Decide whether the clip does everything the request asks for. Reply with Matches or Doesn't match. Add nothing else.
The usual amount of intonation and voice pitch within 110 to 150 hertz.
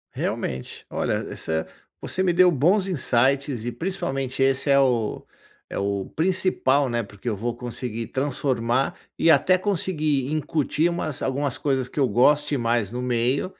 Matches